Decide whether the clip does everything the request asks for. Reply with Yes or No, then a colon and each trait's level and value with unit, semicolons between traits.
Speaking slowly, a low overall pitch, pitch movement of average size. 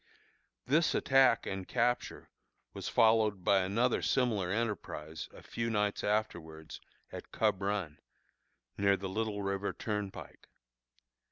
Yes: slow, 115 wpm; low, 105 Hz; average, 3.0 semitones